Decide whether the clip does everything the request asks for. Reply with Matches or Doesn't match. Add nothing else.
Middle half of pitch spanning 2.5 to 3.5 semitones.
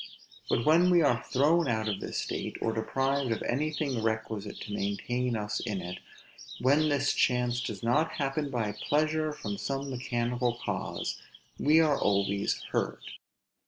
Doesn't match